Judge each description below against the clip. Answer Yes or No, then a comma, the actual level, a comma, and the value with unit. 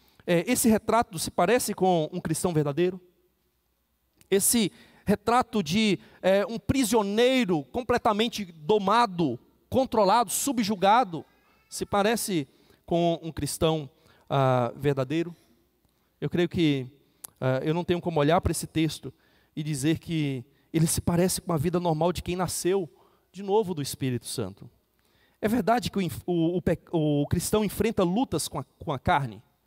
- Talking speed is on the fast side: No, average, 140 wpm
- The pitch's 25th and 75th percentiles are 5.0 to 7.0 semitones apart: Yes, average, 5.3 semitones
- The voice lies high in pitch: No, medium, 175 Hz